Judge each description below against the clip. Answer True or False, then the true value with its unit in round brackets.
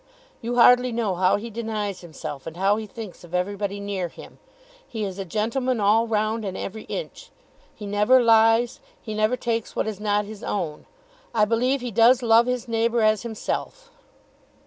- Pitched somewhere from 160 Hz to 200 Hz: False (220 Hz)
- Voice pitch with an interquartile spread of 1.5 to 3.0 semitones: True (2.6 semitones)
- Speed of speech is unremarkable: True (180 wpm)